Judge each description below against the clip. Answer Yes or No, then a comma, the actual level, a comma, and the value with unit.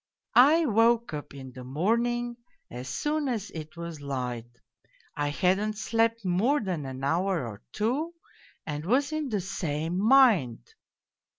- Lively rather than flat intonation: Yes, wide, 8.4 semitones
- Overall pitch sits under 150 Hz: No, high, 190 Hz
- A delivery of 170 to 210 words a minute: No, average, 140 wpm